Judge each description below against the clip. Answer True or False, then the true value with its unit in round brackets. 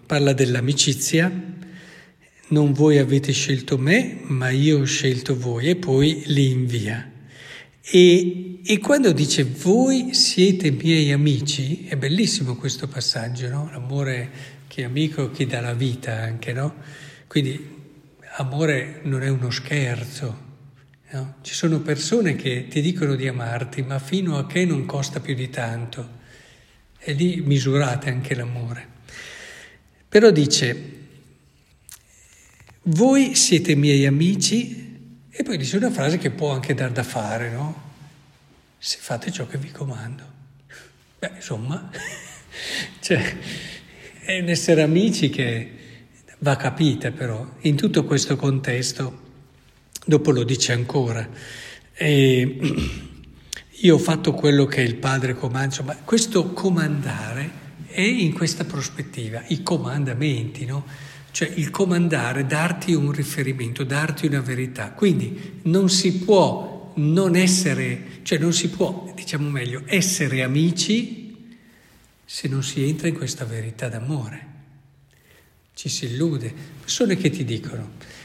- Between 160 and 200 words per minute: False (130 wpm)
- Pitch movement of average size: True (4.0 semitones)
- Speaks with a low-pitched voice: False (145 Hz)